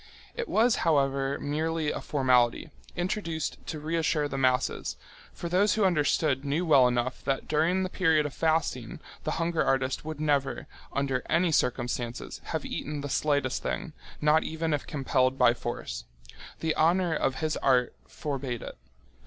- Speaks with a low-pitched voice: No, medium, 150 Hz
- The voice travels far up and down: No, average, 3.4 semitones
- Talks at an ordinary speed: Yes, average, 155 wpm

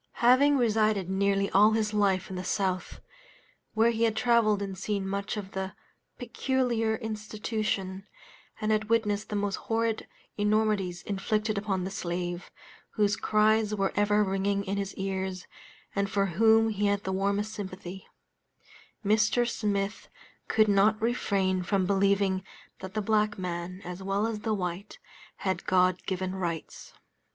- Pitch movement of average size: No, narrow, 2.1 semitones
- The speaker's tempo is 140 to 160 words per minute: Yes, average, 145 wpm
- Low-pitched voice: No, high, 200 Hz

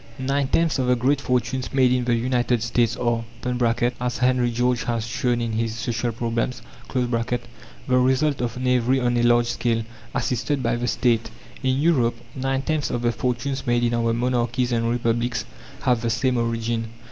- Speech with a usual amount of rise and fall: No, narrow, 1.5 semitones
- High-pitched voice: No, low, 120 Hz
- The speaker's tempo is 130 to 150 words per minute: No, average, 175 wpm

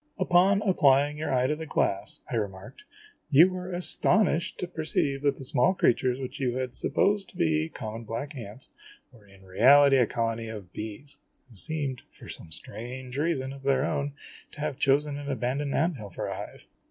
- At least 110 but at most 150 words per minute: No, average, 190 wpm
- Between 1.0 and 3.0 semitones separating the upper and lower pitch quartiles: No, average, 4.7 semitones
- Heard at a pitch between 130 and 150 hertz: Yes, low, 135 Hz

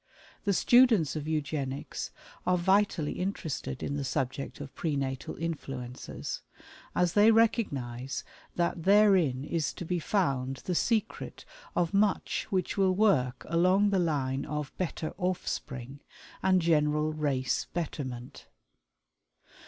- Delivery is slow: Yes, slow, 120 wpm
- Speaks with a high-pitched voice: No, medium, 160 Hz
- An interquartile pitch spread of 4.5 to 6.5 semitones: Yes, wide, 5.5 semitones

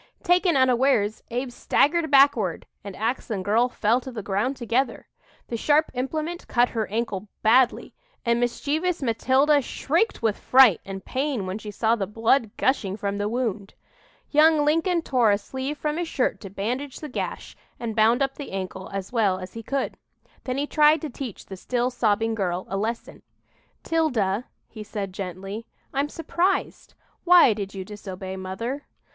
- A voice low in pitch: No, high, 240 Hz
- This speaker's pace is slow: No, average, 170 wpm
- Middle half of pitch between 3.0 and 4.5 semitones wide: No, wide, 5.4 semitones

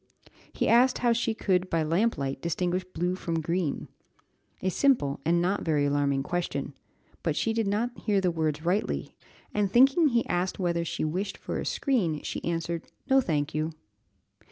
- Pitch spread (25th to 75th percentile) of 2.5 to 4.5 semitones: No, average, 5.0 semitones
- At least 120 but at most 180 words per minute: Yes, average, 170 wpm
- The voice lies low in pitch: No, medium, 180 Hz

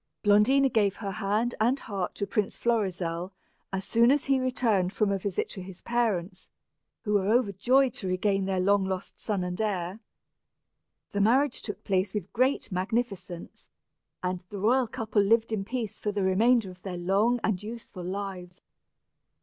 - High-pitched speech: Yes, high, 205 Hz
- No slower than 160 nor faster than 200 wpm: Yes, average, 165 wpm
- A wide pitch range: No, average, 3.4 semitones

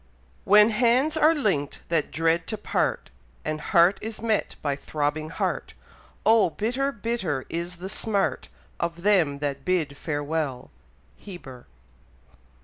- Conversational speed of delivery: No, slow, 130 wpm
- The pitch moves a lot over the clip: Yes, wide, 6.2 semitones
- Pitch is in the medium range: Yes, medium, 175 Hz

